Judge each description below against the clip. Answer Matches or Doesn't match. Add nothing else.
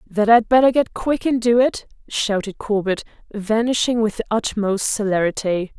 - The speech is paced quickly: Doesn't match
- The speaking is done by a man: Doesn't match